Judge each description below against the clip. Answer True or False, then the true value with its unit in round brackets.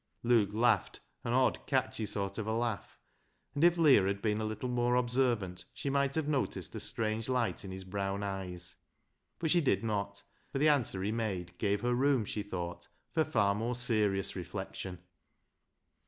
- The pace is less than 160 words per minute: False (180 wpm)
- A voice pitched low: True (110 Hz)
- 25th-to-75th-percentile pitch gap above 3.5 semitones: True (4.0 semitones)